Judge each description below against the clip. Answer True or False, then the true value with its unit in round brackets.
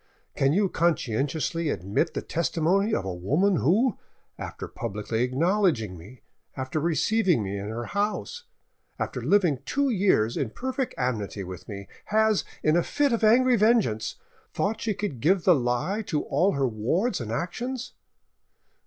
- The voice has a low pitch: False (165 Hz)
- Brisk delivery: False (155 wpm)